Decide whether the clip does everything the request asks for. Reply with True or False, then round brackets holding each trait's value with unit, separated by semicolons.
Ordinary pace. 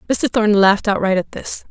False (210 wpm)